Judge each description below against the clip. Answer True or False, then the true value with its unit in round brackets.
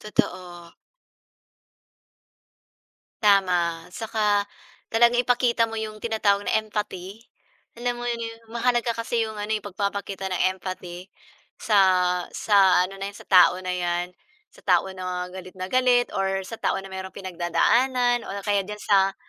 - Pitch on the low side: False (200 Hz)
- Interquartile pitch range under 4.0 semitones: True (3.6 semitones)